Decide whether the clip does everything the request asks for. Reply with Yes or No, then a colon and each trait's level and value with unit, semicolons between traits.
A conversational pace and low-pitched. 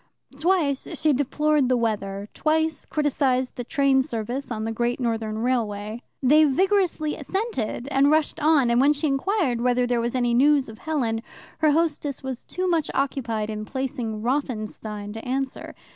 No: average, 160 wpm; very high, 265 Hz